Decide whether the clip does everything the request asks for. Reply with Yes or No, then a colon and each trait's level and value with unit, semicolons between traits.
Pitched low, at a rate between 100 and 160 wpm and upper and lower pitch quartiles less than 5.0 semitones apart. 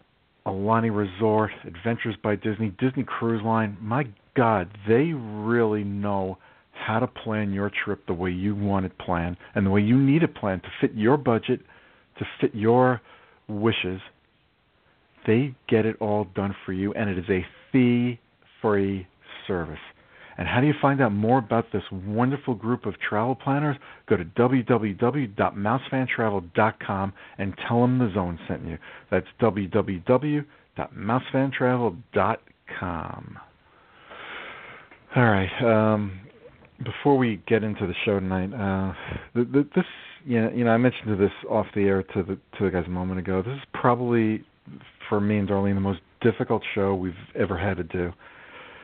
Yes: low, 110 Hz; average, 155 wpm; average, 3.8 semitones